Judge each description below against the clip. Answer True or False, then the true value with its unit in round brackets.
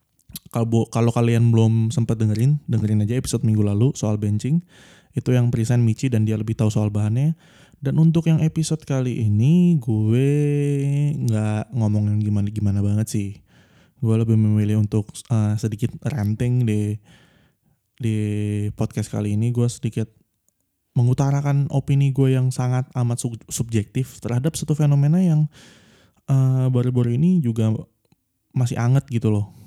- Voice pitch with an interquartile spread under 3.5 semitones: False (4.2 semitones)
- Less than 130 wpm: False (140 wpm)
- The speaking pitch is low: True (120 Hz)